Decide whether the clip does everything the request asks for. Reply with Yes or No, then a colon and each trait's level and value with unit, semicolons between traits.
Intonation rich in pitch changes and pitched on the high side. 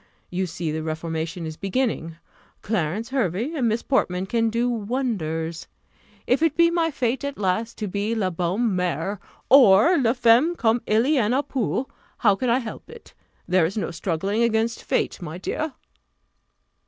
Yes: wide, 5.7 semitones; high, 220 Hz